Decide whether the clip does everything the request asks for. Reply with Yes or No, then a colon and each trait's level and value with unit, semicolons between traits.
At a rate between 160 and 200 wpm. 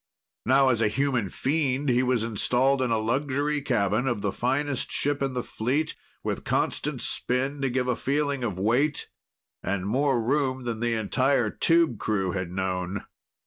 Yes: average, 170 wpm